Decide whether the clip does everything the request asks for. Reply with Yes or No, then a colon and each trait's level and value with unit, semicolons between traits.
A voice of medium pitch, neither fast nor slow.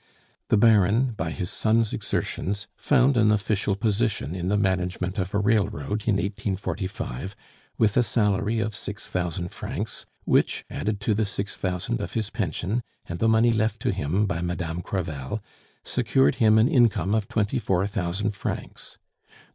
No: low, 100 Hz; average, 160 wpm